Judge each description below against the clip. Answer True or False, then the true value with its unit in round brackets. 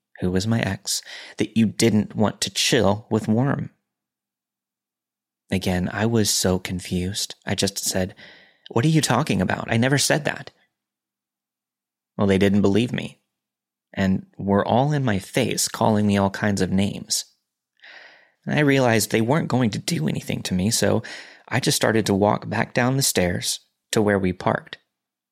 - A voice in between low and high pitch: False (100 Hz)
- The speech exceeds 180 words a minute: False (170 wpm)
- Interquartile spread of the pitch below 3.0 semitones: False (3.8 semitones)